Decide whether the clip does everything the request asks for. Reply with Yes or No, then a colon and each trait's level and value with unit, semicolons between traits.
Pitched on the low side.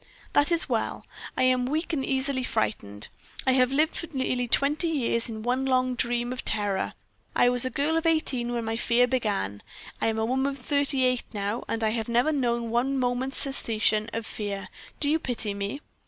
No: very high, 250 Hz